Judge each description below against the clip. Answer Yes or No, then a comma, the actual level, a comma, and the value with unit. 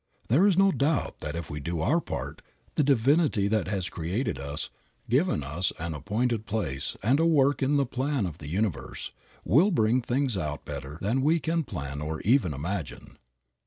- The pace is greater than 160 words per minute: Yes, average, 185 wpm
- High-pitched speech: No, low, 110 Hz